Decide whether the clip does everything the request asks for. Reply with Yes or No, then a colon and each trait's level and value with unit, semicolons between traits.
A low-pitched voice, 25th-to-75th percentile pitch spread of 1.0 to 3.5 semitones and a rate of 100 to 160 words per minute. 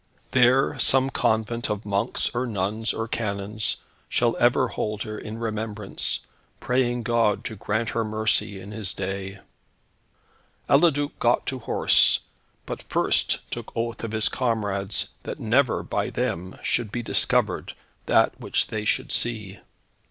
Yes: low, 110 Hz; narrow, 2.5 semitones; average, 140 wpm